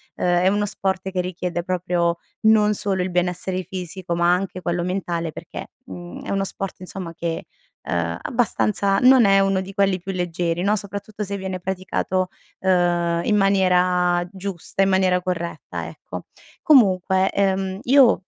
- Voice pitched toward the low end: No, medium, 185 Hz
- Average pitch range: No, narrow, 1.8 semitones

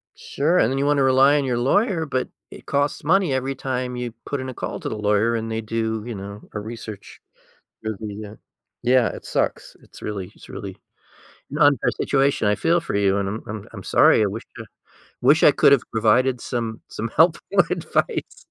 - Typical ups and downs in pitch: Yes, average, 4.4 semitones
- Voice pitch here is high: No, low, 125 Hz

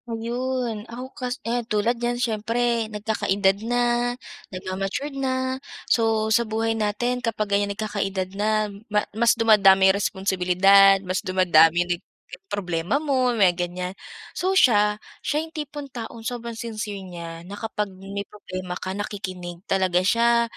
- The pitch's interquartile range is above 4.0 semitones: No, average, 3.7 semitones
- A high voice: Yes, high, 210 Hz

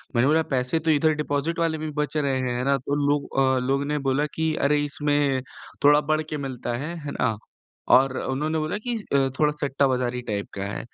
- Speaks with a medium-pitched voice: Yes, medium, 145 Hz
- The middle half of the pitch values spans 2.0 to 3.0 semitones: Yes, average, 2.7 semitones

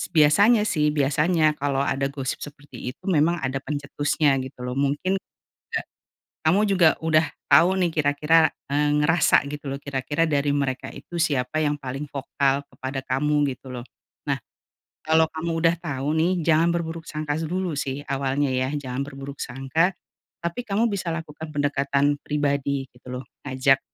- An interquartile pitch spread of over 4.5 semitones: No, average, 2.9 semitones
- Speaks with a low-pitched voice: No, medium, 145 Hz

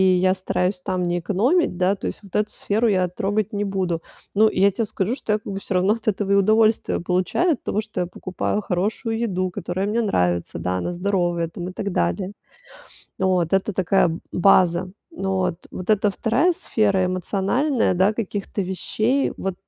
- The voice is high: Yes, high, 195 Hz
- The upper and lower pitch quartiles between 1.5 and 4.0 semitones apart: Yes, average, 2.8 semitones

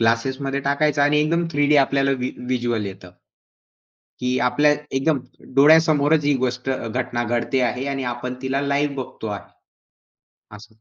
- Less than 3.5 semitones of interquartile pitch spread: Yes, average, 2.7 semitones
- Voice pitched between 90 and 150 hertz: Yes, low, 135 Hz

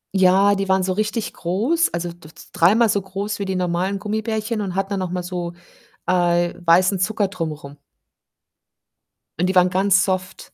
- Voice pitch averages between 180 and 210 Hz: Yes, medium, 185 Hz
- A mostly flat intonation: Yes, narrow, 2.2 semitones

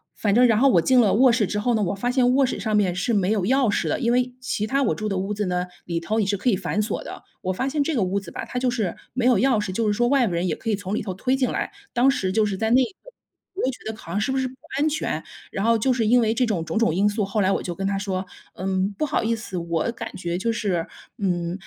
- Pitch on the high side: Yes, high, 215 Hz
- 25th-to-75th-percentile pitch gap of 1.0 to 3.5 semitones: No, average, 4.4 semitones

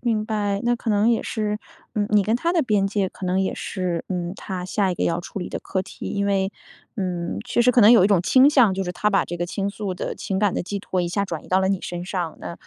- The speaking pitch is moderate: No, high, 195 Hz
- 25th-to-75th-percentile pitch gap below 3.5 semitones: Yes, narrow, 2.6 semitones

